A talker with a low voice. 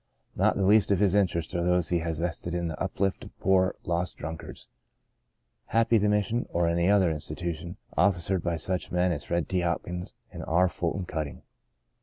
Yes: very low, 90 Hz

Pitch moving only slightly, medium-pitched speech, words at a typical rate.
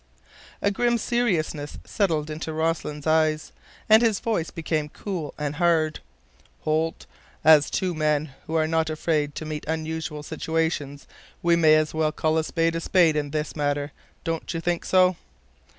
Yes: narrow, 1.5 semitones; medium, 160 Hz; average, 160 wpm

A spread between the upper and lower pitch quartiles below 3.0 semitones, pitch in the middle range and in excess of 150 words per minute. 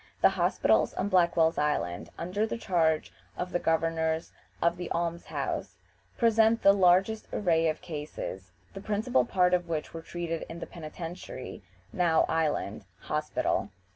No: narrow, 2.5 semitones; medium, 170 Hz; average, 145 wpm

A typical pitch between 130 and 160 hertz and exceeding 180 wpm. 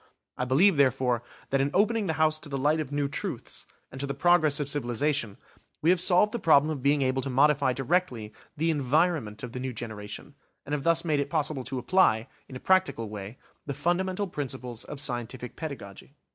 Yes: medium, 140 Hz; average, 200 wpm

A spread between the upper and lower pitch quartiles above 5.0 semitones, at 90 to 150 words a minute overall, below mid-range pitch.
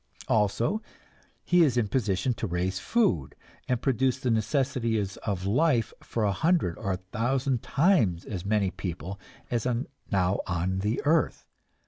Yes: wide, 5.5 semitones; average, 145 wpm; low, 110 Hz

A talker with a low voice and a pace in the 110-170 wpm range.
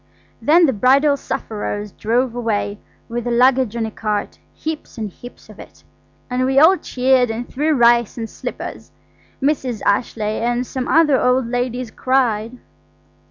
No: high, 245 Hz; average, 150 wpm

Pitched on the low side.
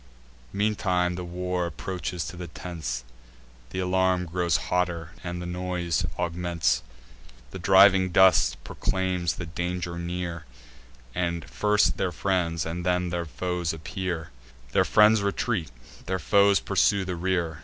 Yes: very low, 90 Hz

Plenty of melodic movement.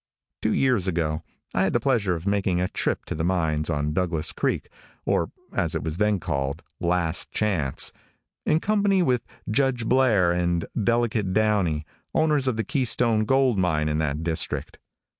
Yes: wide, 6.6 semitones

